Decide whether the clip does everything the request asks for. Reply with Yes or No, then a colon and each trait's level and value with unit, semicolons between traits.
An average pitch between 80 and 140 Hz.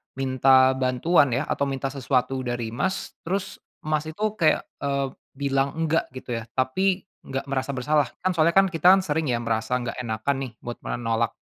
Yes: low, 135 Hz